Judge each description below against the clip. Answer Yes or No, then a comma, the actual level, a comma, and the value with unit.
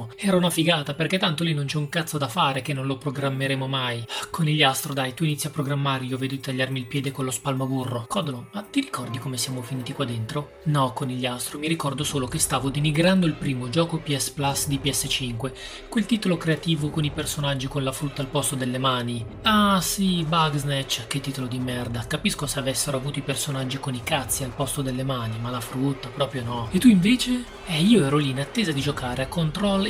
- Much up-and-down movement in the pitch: No, average, 3.3 semitones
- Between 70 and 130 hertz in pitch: No, medium, 140 Hz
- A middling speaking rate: No, fast, 215 wpm